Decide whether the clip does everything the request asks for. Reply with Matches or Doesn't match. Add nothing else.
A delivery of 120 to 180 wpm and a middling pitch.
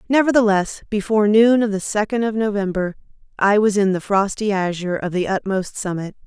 Doesn't match